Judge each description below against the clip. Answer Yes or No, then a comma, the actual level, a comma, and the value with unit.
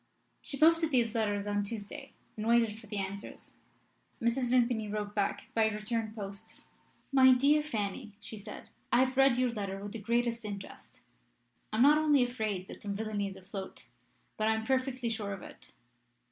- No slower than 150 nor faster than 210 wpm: Yes, average, 180 wpm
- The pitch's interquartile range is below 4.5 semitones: Yes, average, 3.2 semitones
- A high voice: Yes, high, 220 Hz